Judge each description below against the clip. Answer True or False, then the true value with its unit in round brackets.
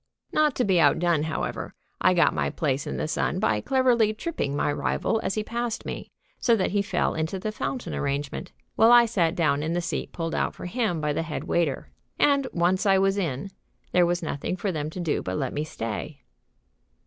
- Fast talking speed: True (210 wpm)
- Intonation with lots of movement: True (5.8 semitones)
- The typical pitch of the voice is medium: True (175 Hz)